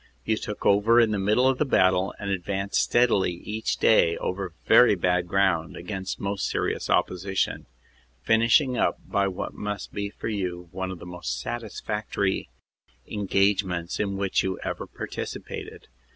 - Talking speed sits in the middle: Yes, average, 155 wpm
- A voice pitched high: No, low, 100 Hz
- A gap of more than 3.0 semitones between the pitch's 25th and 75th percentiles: No, narrow, 2.5 semitones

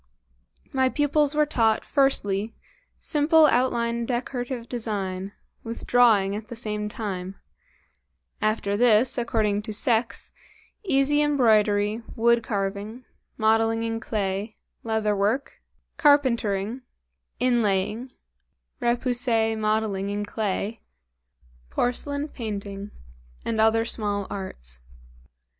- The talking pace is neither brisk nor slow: No, slow, 95 wpm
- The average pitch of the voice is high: Yes, high, 225 Hz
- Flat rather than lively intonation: No, average, 3.0 semitones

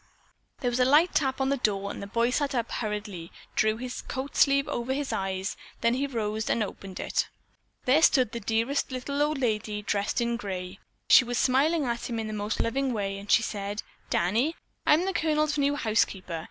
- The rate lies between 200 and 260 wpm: Yes, fast, 205 wpm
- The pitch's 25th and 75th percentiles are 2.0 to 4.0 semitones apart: No, average, 4.8 semitones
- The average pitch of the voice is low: No, high, 235 Hz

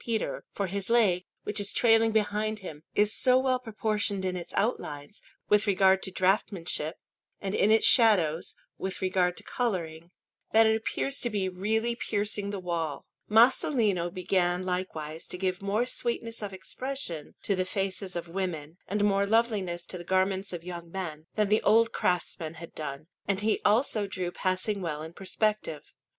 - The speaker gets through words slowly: No, average, 170 wpm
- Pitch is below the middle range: No, high, 195 Hz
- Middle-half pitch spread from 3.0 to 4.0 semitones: Yes, average, 3.4 semitones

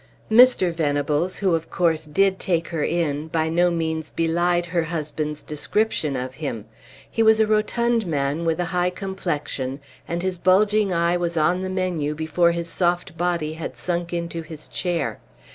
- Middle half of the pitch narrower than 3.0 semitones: Yes, narrow, 2.5 semitones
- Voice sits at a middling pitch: Yes, medium, 170 Hz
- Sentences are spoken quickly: No, average, 170 wpm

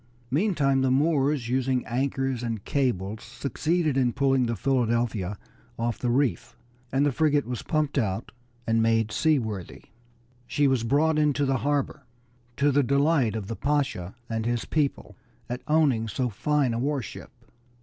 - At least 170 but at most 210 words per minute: No, average, 155 wpm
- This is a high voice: No, low, 130 Hz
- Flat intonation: No, average, 3.8 semitones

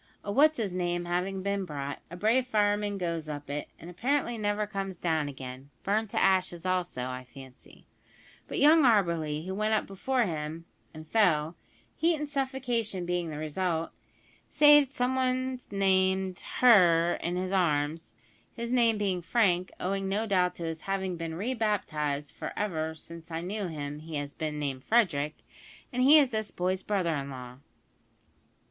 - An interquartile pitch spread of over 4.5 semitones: Yes, average, 5.2 semitones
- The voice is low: No, medium, 185 Hz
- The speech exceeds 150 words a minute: Yes, average, 170 wpm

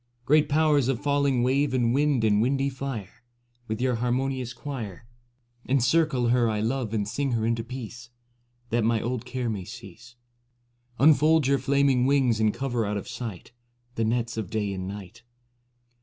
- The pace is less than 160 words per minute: No, average, 170 wpm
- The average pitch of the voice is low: Yes, low, 120 Hz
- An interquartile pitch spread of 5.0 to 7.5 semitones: No, average, 3.4 semitones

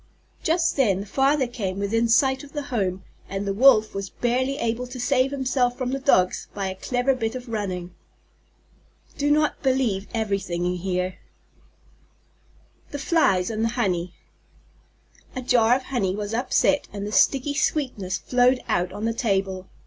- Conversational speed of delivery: Yes, average, 165 wpm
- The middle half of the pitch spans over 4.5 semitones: Yes, average, 5.2 semitones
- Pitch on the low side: No, high, 230 Hz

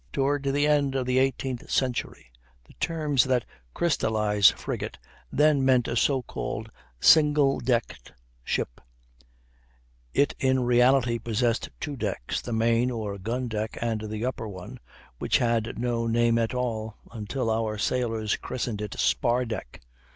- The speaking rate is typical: Yes, average, 145 wpm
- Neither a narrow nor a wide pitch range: Yes, average, 3.0 semitones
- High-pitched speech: No, low, 120 Hz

